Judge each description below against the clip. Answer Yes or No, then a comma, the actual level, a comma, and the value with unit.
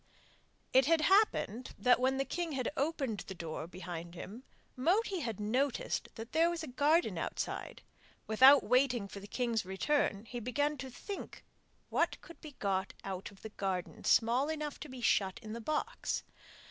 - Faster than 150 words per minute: Yes, average, 165 wpm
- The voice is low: No, very high, 250 Hz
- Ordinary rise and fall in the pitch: No, wide, 6.5 semitones